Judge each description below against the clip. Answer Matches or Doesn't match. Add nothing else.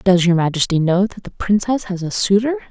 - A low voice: Doesn't match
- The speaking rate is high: Matches